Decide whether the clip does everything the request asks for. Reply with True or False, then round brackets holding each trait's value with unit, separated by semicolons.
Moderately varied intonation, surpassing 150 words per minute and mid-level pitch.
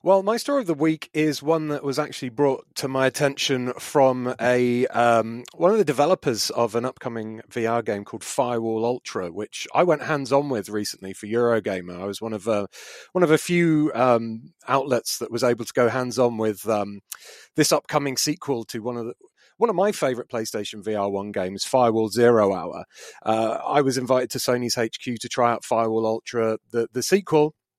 False (4.0 semitones; 200 wpm; 125 Hz)